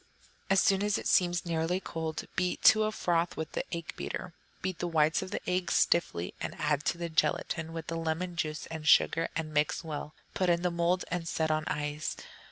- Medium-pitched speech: Yes, medium, 165 Hz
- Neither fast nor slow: No, fast, 210 wpm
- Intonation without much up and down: Yes, narrow, 2.2 semitones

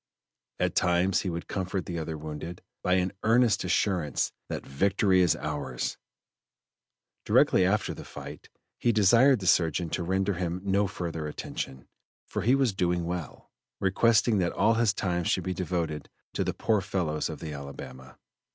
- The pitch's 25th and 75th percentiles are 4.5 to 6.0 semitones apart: No, average, 3.4 semitones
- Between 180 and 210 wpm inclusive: No, average, 160 wpm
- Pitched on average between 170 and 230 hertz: No, very low, 90 Hz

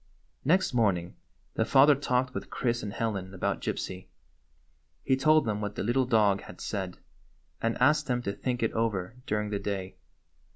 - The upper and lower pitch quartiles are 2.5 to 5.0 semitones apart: Yes, average, 4.2 semitones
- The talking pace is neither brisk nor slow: Yes, average, 170 wpm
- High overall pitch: No, low, 115 Hz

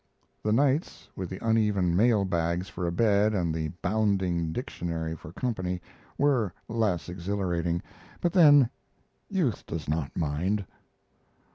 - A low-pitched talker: Yes, very low, 95 Hz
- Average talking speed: No, slow, 130 wpm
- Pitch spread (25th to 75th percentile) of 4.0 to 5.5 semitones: Yes, average, 4.5 semitones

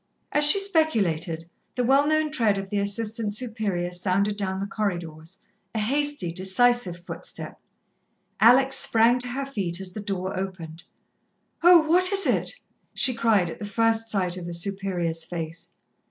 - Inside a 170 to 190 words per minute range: No, average, 155 wpm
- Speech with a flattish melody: No, wide, 5.5 semitones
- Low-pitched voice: No, high, 205 Hz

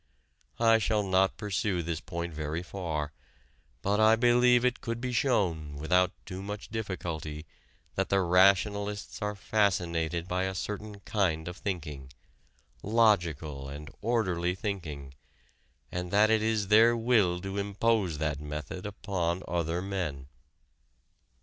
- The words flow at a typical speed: No, slow, 130 wpm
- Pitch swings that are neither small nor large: Yes, average, 4.0 semitones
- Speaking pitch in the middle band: No, very low, 95 Hz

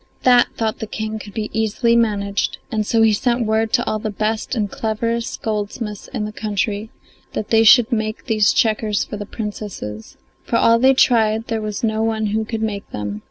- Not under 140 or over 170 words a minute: No, average, 200 wpm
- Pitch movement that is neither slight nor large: No, narrow, 1.2 semitones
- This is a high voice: Yes, high, 220 Hz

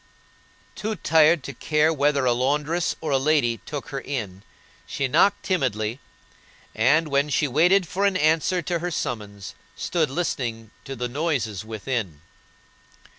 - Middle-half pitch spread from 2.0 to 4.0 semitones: No, average, 5.2 semitones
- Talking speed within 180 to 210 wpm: No, average, 145 wpm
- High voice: No, medium, 140 Hz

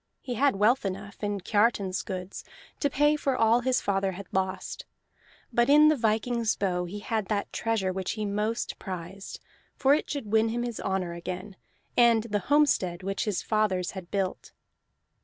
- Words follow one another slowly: No, average, 175 wpm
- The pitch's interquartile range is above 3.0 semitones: Yes, average, 3.8 semitones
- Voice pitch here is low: No, high, 210 Hz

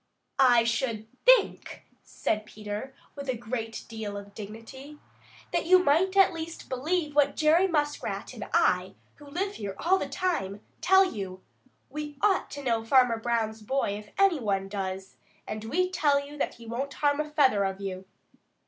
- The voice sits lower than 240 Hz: No, very high, 265 Hz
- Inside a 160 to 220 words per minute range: Yes, average, 170 wpm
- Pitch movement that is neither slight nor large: No, wide, 6.2 semitones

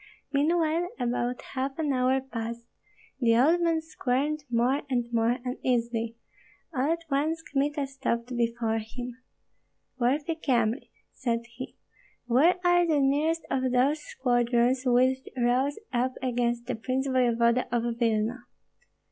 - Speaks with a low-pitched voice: No, very high, 255 Hz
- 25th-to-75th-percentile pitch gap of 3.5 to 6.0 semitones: No, average, 3.1 semitones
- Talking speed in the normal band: No, slow, 130 wpm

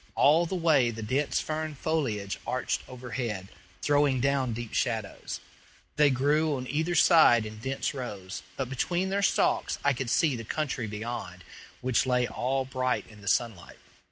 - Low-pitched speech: Yes, low, 130 Hz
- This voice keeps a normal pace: Yes, average, 160 wpm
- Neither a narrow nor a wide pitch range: Yes, average, 4.1 semitones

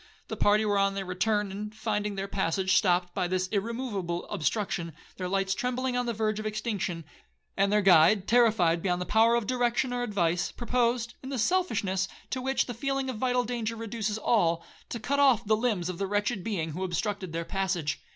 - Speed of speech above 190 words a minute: Yes, average, 200 wpm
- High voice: Yes, high, 210 Hz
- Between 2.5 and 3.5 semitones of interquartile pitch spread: No, average, 4.0 semitones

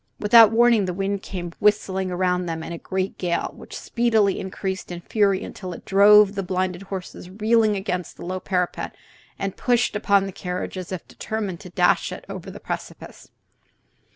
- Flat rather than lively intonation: Yes, narrow, 2.3 semitones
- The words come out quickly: No, average, 180 wpm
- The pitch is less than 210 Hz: Yes, high, 190 Hz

